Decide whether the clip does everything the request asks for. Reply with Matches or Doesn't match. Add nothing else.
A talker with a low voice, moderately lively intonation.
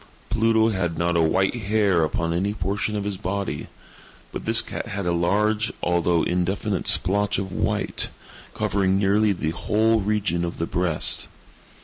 Matches